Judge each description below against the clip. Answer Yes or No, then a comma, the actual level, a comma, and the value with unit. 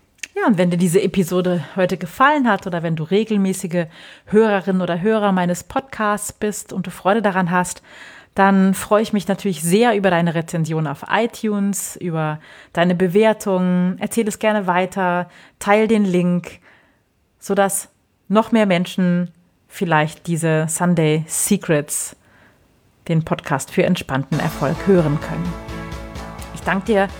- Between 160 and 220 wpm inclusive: No, average, 140 wpm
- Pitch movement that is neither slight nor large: Yes, average, 3.2 semitones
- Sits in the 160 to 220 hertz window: Yes, medium, 185 Hz